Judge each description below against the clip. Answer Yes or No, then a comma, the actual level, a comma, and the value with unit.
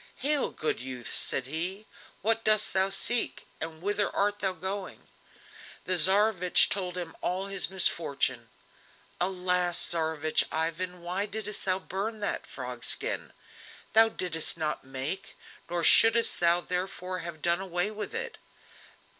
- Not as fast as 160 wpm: Yes, average, 140 wpm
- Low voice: No, medium, 185 Hz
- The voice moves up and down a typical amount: Yes, average, 3.4 semitones